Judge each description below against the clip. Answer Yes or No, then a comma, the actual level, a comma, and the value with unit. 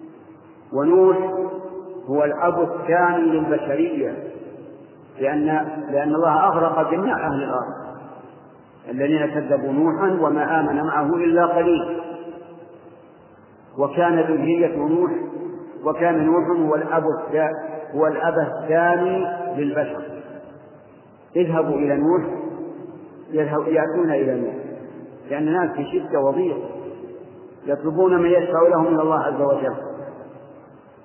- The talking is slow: No, average, 95 wpm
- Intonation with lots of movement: No, narrow, 2.4 semitones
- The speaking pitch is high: No, medium, 165 Hz